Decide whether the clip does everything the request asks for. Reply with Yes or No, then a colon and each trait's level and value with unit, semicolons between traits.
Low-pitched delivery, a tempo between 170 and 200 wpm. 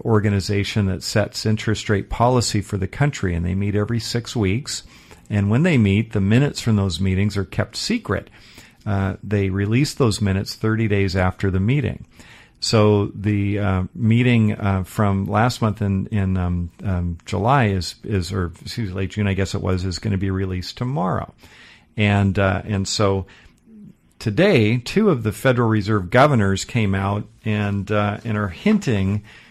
Yes: low, 105 Hz; average, 175 wpm